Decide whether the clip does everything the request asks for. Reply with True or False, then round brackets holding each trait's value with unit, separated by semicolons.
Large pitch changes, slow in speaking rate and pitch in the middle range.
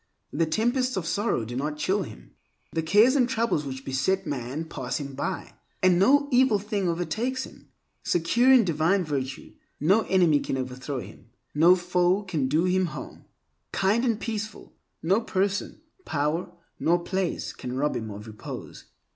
False (6.1 semitones; 160 wpm; 175 Hz)